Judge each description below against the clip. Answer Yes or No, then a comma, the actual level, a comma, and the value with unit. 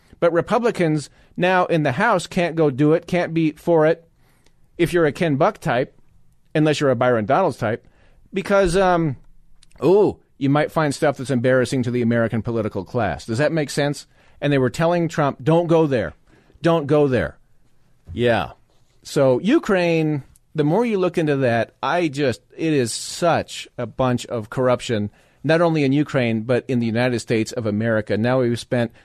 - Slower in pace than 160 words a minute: No, average, 180 wpm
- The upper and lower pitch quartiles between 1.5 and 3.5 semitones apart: No, average, 5.2 semitones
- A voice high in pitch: No, medium, 140 Hz